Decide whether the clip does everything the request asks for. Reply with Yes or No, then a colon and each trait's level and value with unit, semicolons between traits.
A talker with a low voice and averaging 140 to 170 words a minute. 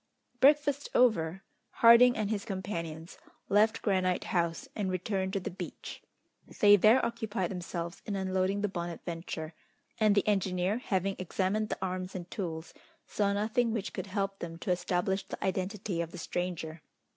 No: high, 190 Hz; average, 155 wpm